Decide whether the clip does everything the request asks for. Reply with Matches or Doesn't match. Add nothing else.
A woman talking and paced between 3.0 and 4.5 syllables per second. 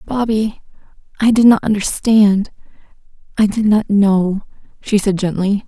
Matches